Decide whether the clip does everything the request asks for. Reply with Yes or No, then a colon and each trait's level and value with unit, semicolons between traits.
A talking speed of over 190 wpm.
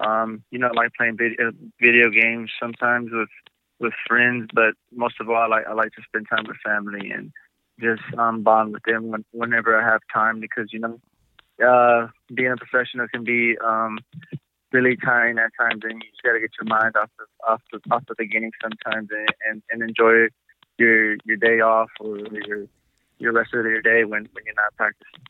Yes: average, 200 wpm